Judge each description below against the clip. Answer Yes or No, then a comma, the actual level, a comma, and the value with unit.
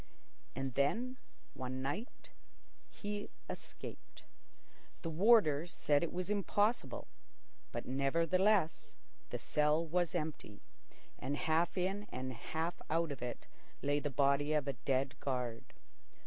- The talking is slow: Yes, slow, 120 wpm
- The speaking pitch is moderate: Yes, medium, 155 Hz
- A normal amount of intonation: Yes, average, 4.8 semitones